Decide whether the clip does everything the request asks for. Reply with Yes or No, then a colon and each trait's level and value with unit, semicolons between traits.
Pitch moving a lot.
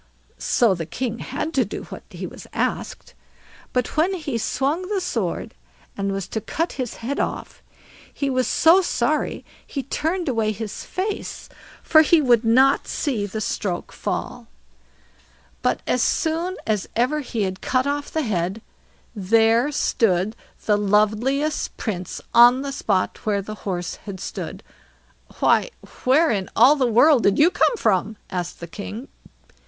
Yes: wide, 5.9 semitones